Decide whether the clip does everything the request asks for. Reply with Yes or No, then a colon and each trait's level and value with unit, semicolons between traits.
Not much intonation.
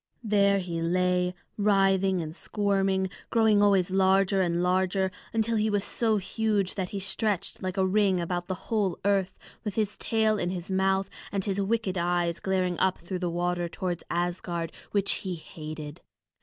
Yes: narrow, 2.2 semitones